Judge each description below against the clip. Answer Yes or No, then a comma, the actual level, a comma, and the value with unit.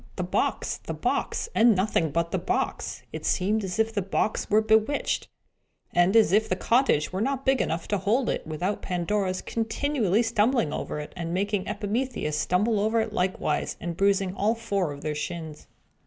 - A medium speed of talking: Yes, average, 185 wpm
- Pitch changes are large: No, average, 3.8 semitones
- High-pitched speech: Yes, high, 200 Hz